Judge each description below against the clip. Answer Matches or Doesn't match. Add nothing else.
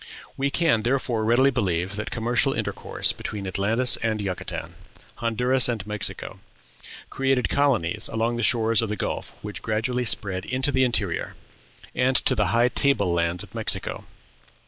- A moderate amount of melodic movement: Matches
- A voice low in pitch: Matches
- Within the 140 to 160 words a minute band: Matches